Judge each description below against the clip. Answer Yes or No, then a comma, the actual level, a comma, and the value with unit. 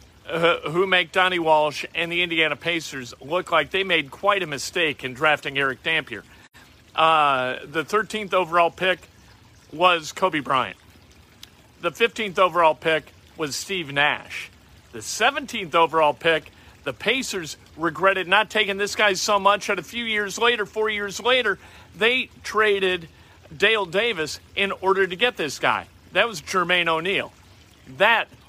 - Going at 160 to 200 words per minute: No, average, 150 wpm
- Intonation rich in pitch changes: No, average, 4.9 semitones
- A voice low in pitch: No, medium, 175 Hz